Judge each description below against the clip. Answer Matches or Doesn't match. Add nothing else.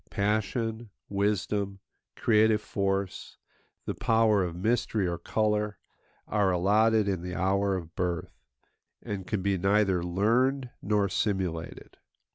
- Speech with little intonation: Matches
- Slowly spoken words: Matches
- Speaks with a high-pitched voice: Doesn't match